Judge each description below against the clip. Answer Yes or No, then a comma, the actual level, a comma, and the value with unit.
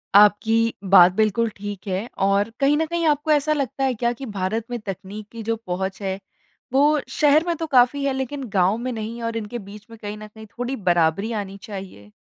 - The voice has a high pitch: Yes, high, 220 Hz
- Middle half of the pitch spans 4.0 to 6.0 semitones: Yes, average, 5.0 semitones